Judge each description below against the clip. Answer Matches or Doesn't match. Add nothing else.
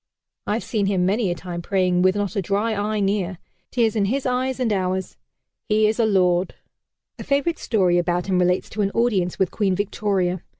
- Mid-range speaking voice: Doesn't match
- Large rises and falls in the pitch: Doesn't match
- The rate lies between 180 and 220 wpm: Matches